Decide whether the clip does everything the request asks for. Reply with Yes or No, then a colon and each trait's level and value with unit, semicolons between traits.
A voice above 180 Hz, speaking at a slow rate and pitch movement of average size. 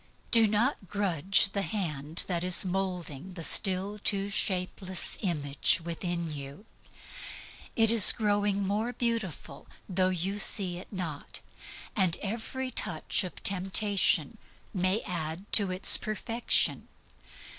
Yes: high, 190 Hz; slow, 120 wpm; average, 3.0 semitones